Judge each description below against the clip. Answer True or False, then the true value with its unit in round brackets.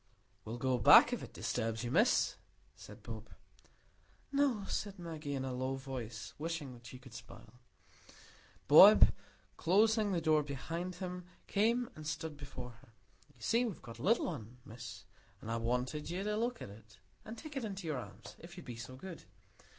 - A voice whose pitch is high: False (150 Hz)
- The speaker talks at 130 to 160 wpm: False (180 wpm)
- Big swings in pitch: True (7.7 semitones)